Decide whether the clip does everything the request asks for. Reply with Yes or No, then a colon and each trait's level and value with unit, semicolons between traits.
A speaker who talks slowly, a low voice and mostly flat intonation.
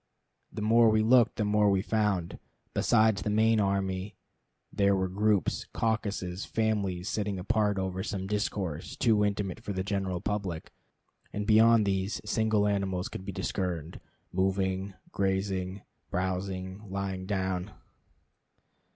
Yes: slow, 130 wpm; low, 100 Hz; narrow, 2.0 semitones